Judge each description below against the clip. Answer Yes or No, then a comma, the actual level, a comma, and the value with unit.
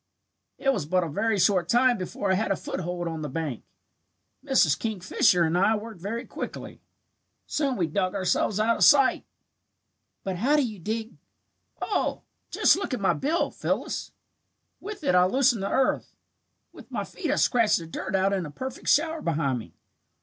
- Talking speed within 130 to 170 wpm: No, average, 185 wpm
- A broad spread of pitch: Yes, wide, 6.3 semitones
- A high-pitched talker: Yes, high, 200 Hz